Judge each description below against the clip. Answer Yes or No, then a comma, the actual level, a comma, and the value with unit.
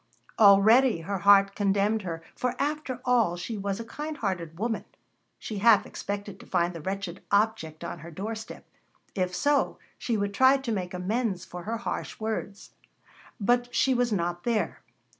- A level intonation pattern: No, average, 4.0 semitones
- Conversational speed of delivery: Yes, average, 165 wpm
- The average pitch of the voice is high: Yes, high, 205 Hz